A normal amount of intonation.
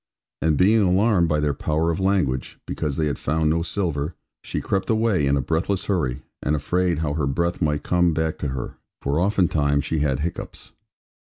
Yes: average, 3.8 semitones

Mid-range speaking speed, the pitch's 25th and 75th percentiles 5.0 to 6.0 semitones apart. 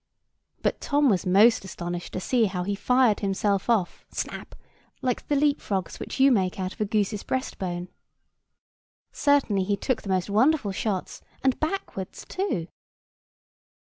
Yes: average, 150 wpm; wide, 5.5 semitones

